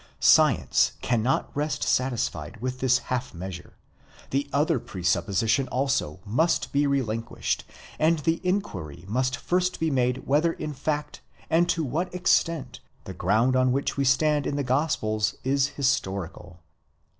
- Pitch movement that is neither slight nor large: Yes, average, 4.8 semitones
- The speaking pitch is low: Yes, low, 130 Hz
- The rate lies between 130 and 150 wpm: Yes, average, 140 wpm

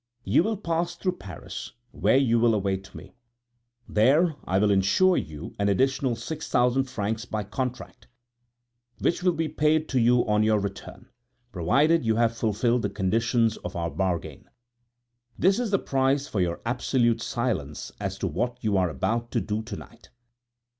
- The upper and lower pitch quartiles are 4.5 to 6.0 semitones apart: Yes, average, 5.1 semitones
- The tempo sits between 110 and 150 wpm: No, average, 165 wpm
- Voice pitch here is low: Yes, low, 115 Hz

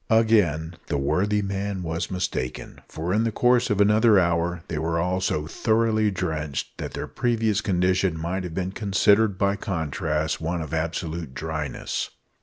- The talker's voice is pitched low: Yes, very low, 90 Hz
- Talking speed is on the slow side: No, average, 160 wpm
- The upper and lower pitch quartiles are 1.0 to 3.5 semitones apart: No, average, 4.3 semitones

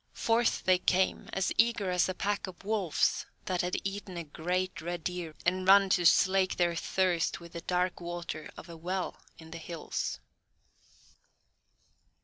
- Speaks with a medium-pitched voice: Yes, medium, 180 Hz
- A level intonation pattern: Yes, narrow, 1.8 semitones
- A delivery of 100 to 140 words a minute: No, average, 160 wpm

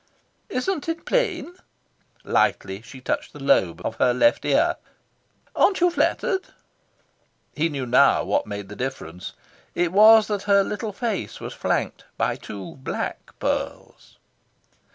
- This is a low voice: No, medium, 175 Hz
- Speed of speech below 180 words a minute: Yes, slow, 135 wpm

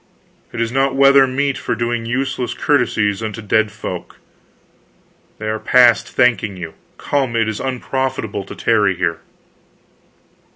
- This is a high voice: No, low, 115 Hz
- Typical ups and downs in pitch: Yes, average, 3.7 semitones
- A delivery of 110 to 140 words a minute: Yes, slow, 135 wpm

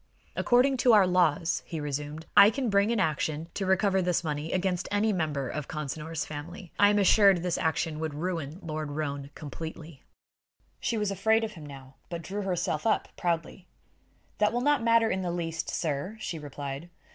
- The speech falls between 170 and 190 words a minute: Yes, average, 185 wpm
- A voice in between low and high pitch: Yes, medium, 170 Hz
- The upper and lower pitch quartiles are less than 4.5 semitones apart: No, average, 4.8 semitones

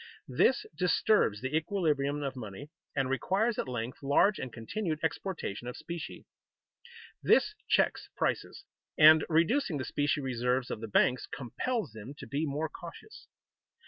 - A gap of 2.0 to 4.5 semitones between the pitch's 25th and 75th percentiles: No, average, 5.0 semitones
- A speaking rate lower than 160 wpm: Yes, average, 145 wpm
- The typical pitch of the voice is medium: Yes, medium, 145 Hz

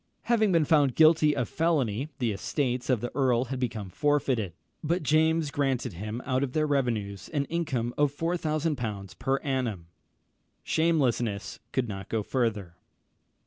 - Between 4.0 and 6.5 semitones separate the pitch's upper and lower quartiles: Yes, average, 5.2 semitones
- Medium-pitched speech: No, low, 130 Hz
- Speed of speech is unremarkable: Yes, average, 145 wpm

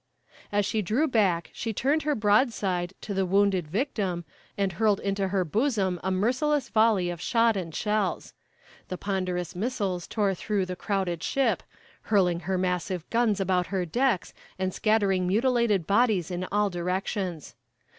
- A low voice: No, high, 195 Hz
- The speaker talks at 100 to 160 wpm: Yes, average, 155 wpm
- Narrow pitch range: No, average, 3.2 semitones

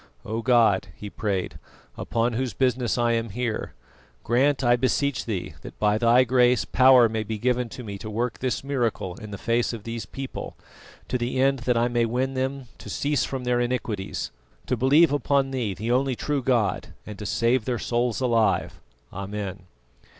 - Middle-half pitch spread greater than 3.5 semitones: No, average, 2.8 semitones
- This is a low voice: Yes, low, 120 Hz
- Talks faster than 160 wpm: Yes, average, 185 wpm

